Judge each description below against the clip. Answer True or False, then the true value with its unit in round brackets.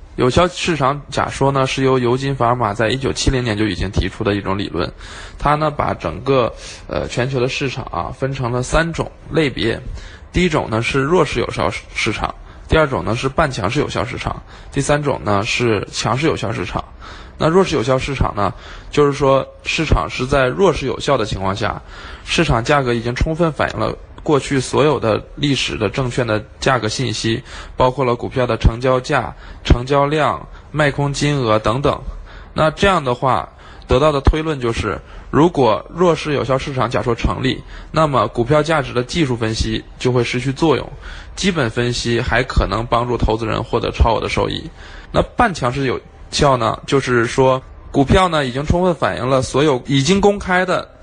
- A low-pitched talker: True (125 Hz)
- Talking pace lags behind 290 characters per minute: True (275 characters per minute)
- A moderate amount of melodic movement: True (4.6 semitones)